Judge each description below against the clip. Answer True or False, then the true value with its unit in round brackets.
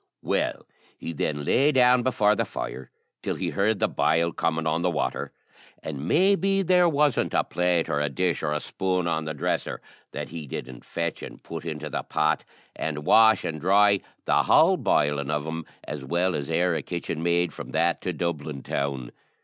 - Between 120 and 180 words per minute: False (190 wpm)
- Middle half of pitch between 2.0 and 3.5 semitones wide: False (4.1 semitones)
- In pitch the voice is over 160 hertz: False (85 Hz)